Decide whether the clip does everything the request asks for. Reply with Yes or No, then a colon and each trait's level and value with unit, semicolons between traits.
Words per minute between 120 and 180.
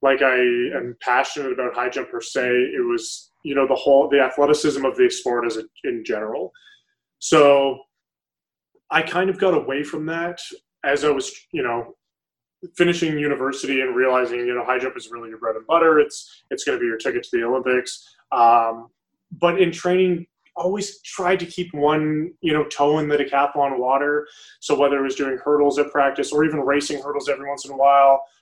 No: average, 195 wpm